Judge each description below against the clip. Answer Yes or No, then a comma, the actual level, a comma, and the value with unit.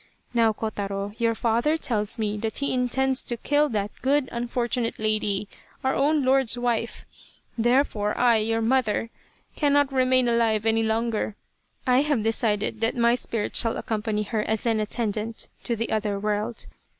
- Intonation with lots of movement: No, average, 2.7 semitones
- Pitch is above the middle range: Yes, high, 230 Hz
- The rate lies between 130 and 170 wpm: Yes, average, 155 wpm